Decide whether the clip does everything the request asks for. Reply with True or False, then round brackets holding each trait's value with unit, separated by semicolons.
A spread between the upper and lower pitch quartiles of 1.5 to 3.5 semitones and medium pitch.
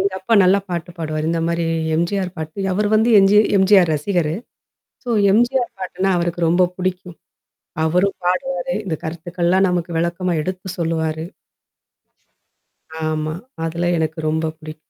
True (3.0 semitones; 175 Hz)